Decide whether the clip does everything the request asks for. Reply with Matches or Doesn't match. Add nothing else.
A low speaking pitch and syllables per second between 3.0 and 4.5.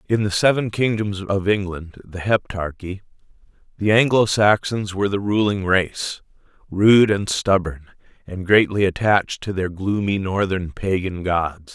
Matches